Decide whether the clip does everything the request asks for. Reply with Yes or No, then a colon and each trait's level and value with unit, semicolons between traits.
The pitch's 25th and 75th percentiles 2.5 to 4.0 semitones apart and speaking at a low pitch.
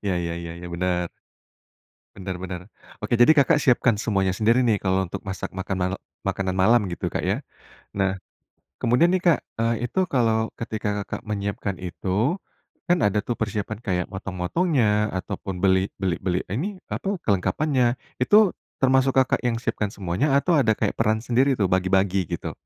No: average, 5.0 semitones; low, 105 Hz